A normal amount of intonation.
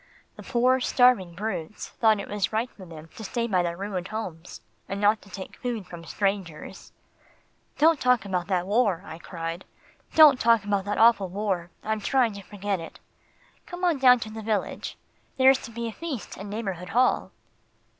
Yes: average, 4.1 semitones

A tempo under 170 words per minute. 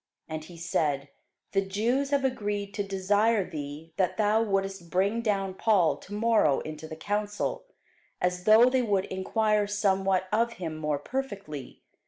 Yes: average, 155 wpm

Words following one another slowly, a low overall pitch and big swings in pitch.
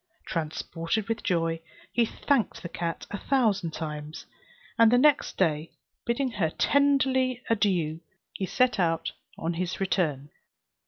No: slow, 130 wpm; medium, 185 Hz; wide, 6.6 semitones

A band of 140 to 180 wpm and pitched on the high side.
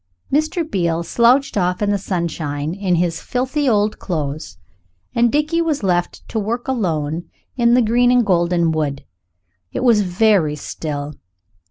Yes: average, 150 wpm; high, 195 Hz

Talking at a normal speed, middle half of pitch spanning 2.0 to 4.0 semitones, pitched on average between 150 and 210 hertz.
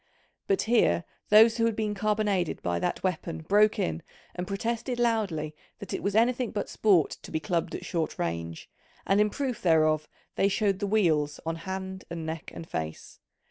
No: average, 180 wpm; average, 5.2 semitones; high, 190 Hz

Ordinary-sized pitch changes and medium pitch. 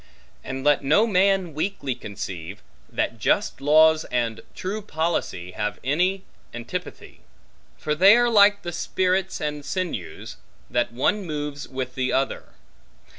No: wide, 6.4 semitones; medium, 155 Hz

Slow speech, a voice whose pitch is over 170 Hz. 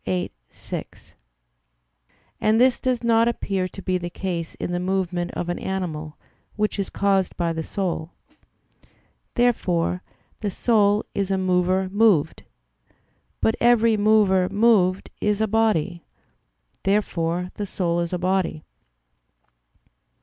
Yes: slow, 130 wpm; high, 190 Hz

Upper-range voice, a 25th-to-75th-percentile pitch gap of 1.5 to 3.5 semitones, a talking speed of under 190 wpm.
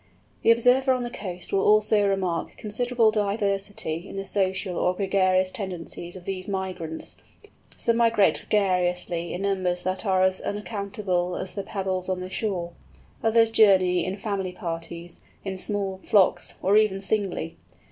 Yes: high, 195 Hz; narrow, 2.4 semitones; average, 150 wpm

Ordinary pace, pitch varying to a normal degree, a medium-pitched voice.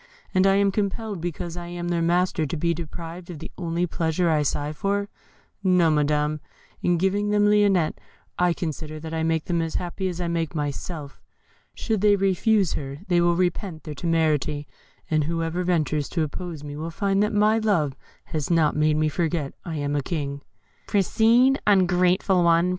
Yes: average, 185 wpm; average, 3.4 semitones; medium, 170 Hz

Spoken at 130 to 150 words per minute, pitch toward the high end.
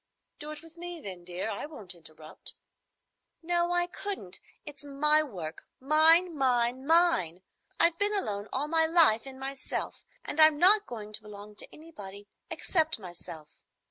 Yes: average, 140 wpm; very high, 280 Hz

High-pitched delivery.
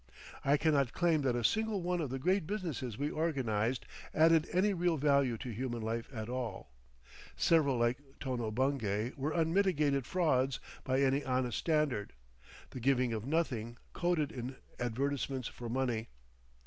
No: low, 135 Hz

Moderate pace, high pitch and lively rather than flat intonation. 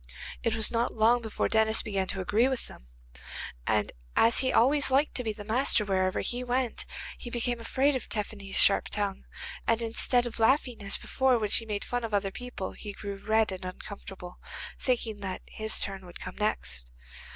No: average, 185 wpm; high, 220 Hz; average, 3.4 semitones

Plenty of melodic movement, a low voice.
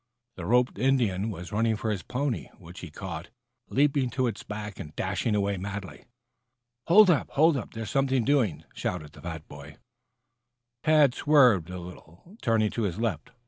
Yes: wide, 6.3 semitones; low, 110 Hz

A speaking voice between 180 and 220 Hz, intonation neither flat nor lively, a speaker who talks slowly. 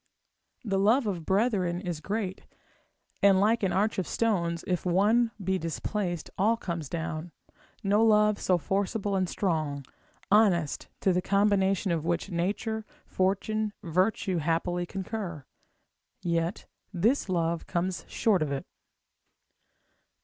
Yes: high, 190 Hz; average, 3.4 semitones; slow, 130 wpm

